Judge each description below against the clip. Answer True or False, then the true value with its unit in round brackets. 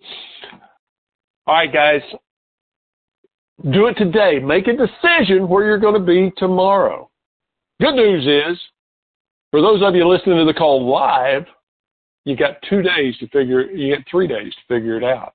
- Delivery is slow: False (165 wpm)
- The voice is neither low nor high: True (180 Hz)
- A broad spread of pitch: True (6.0 semitones)